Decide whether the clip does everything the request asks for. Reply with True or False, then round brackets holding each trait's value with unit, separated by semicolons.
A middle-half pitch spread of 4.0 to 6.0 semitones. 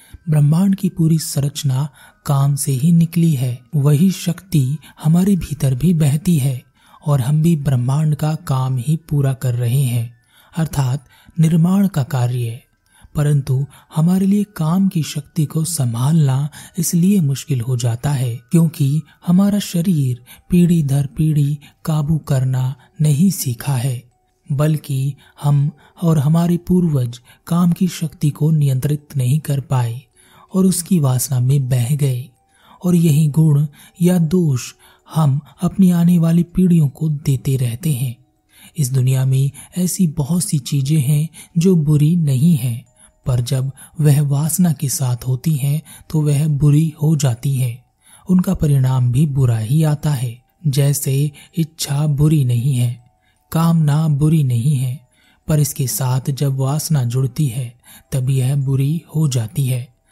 False (3.5 semitones)